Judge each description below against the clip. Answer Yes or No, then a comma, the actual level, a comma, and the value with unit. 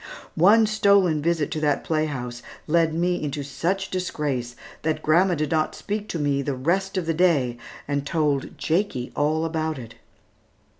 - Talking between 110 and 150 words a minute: No, average, 160 wpm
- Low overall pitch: No, medium, 155 Hz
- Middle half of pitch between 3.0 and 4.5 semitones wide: Yes, average, 3.8 semitones